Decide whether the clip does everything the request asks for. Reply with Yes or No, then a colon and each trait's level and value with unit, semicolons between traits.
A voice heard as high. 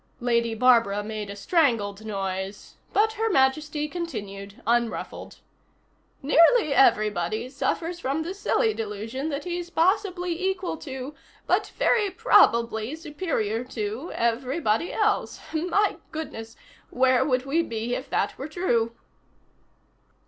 Yes: very high, 265 Hz